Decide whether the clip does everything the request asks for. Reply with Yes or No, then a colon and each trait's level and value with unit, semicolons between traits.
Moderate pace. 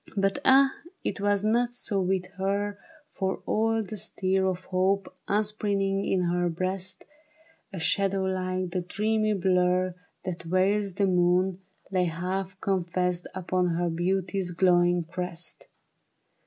No: slow, 130 wpm